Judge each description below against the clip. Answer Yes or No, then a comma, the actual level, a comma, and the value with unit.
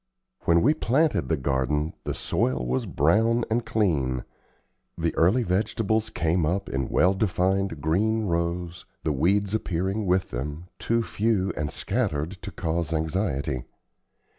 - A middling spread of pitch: No, wide, 5.8 semitones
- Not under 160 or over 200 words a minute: No, average, 140 wpm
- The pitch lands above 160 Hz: No, very low, 90 Hz